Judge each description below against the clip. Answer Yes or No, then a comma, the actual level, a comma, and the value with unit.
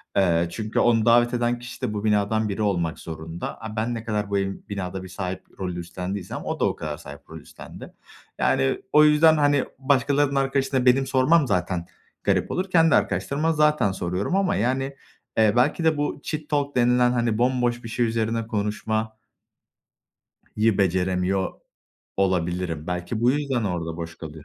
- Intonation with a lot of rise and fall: Yes, wide, 6.0 semitones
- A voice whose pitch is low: Yes, low, 110 Hz